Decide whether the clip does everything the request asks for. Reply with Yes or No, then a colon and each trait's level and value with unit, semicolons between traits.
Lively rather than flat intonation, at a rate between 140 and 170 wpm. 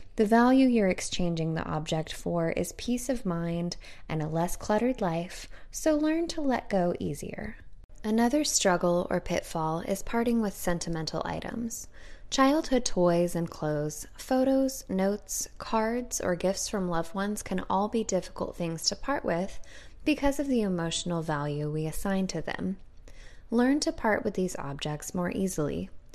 Yes: wide, 5.9 semitones; average, 155 wpm